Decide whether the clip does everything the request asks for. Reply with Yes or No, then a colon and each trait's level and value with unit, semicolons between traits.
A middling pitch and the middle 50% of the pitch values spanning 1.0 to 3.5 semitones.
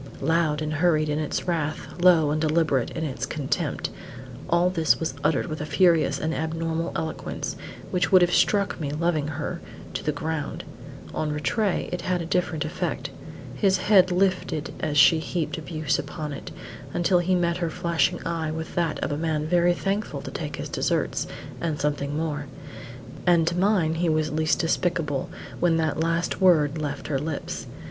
Yes: medium, 160 Hz; narrow, 2.4 semitones